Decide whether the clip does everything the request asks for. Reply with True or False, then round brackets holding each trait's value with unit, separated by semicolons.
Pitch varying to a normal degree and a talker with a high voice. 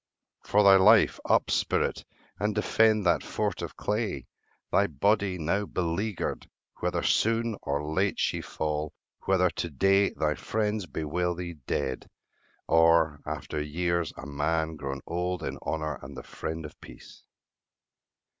False (4.5 semitones; 85 Hz)